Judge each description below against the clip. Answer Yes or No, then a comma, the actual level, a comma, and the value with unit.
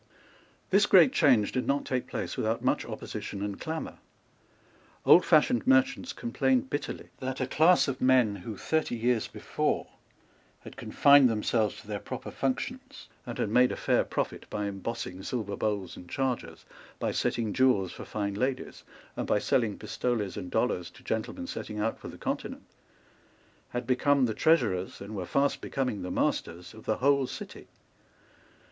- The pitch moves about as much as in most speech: Yes, average, 4.8 semitones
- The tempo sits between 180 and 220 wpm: No, average, 160 wpm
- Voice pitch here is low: Yes, low, 120 Hz